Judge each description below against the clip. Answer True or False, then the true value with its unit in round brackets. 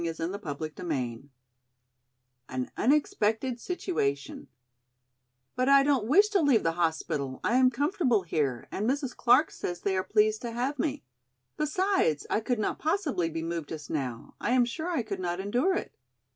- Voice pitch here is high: True (215 Hz)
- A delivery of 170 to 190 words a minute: False (160 wpm)